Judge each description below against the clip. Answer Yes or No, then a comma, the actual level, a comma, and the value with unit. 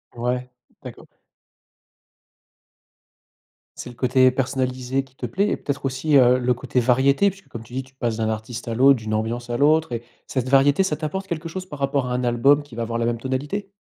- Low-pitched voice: Yes, low, 130 Hz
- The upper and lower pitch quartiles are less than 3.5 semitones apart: Yes, average, 2.8 semitones